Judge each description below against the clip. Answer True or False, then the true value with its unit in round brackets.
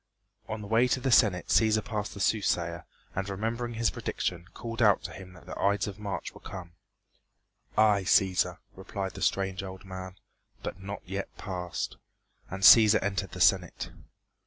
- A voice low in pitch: True (100 Hz)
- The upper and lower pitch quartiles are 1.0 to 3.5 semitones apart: True (2.5 semitones)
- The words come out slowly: False (170 wpm)